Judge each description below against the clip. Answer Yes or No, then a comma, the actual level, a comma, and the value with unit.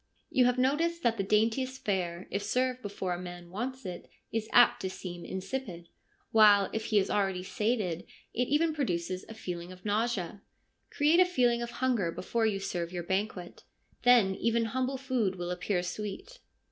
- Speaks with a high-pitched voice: Yes, high, 210 Hz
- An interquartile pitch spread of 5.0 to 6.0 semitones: Yes, average, 5.3 semitones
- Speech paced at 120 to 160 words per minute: No, average, 175 wpm